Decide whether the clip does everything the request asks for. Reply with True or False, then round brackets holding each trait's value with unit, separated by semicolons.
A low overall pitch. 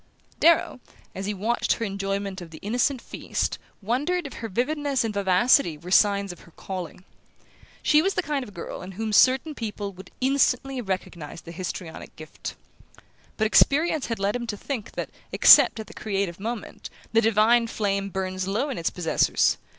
False (210 Hz)